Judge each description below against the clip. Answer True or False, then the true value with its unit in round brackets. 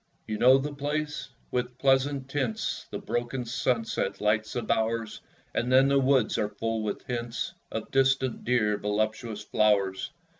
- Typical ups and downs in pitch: True (3.7 semitones)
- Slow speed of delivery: False (150 wpm)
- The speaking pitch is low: True (120 Hz)